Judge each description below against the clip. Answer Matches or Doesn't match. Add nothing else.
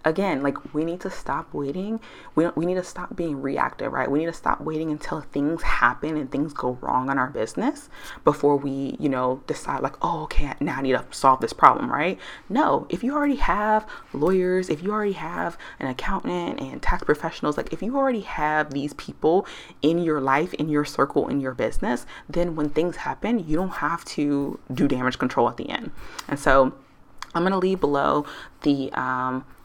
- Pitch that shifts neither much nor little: Matches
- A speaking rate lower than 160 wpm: Doesn't match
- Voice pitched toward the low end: Doesn't match